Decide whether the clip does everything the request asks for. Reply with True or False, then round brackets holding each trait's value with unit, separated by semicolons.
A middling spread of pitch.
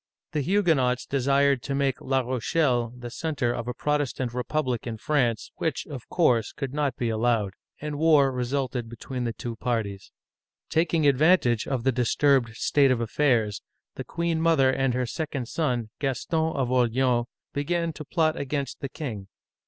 True (3.6 semitones)